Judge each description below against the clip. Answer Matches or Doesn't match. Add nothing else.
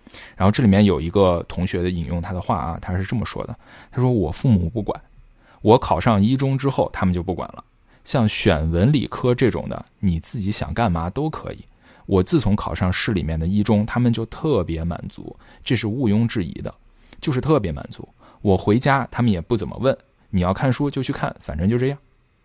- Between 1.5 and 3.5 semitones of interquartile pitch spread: Doesn't match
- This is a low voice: Matches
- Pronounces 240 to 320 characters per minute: Matches